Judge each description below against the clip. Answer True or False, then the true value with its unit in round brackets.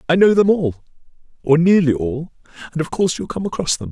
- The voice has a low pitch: False (165 Hz)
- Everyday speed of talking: False (215 wpm)